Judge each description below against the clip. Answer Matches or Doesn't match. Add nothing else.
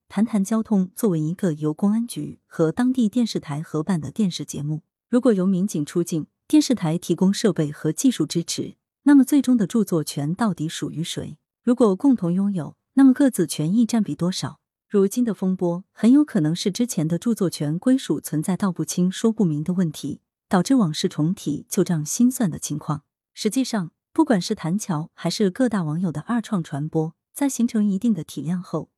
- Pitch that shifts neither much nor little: Doesn't match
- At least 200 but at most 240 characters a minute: Doesn't match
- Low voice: Doesn't match